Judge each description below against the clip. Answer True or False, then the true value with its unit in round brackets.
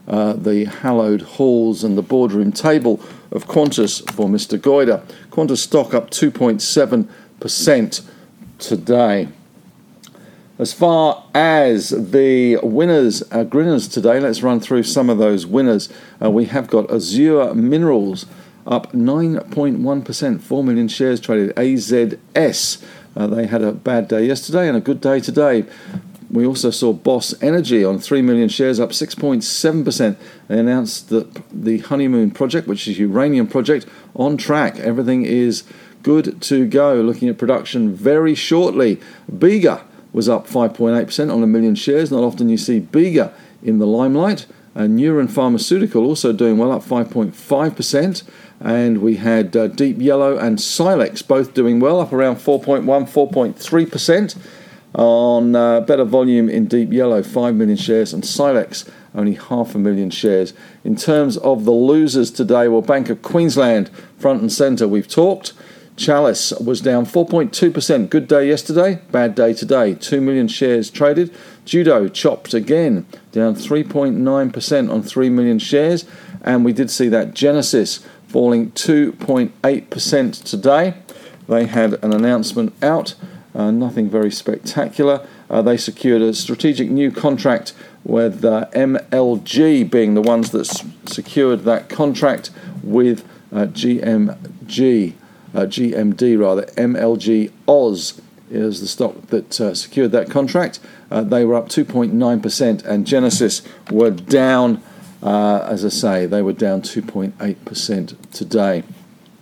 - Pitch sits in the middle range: False (130 Hz)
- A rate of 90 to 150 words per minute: True (140 wpm)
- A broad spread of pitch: True (5.7 semitones)